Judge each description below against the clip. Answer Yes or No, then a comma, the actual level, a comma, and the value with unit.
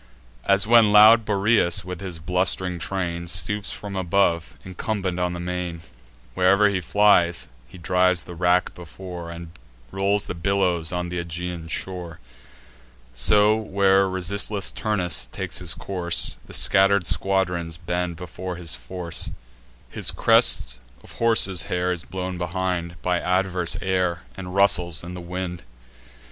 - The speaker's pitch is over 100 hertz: No, very low, 90 Hz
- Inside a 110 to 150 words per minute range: Yes, average, 140 wpm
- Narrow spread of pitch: Yes, narrow, 2.0 semitones